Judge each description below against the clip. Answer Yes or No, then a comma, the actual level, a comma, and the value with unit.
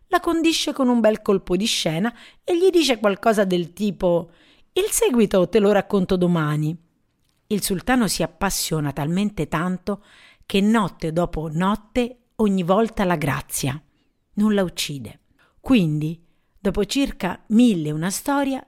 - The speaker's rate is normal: Yes, average, 140 wpm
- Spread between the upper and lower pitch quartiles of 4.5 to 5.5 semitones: Yes, average, 5.2 semitones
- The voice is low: No, high, 200 Hz